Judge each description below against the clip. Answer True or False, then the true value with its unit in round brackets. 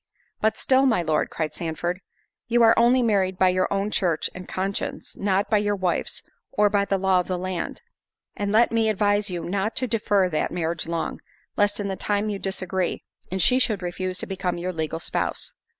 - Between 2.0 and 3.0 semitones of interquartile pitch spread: True (2.6 semitones)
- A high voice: True (195 Hz)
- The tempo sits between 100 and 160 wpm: False (200 wpm)